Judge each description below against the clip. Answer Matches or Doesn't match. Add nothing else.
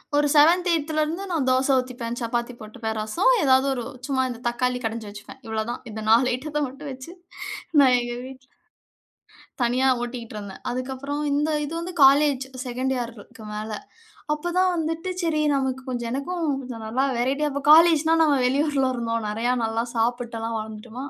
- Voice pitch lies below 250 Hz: Doesn't match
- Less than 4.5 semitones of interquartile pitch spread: Matches